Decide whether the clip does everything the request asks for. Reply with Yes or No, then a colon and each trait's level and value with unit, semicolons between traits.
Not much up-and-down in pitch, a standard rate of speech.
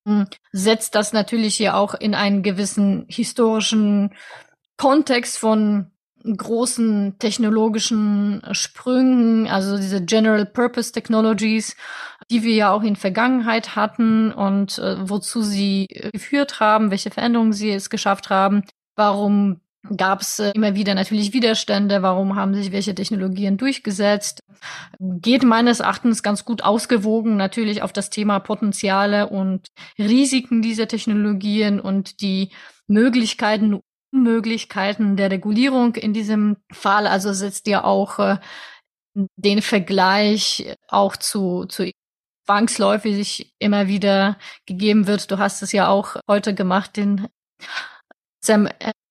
No: narrow, 1.9 semitones; slow, 120 wpm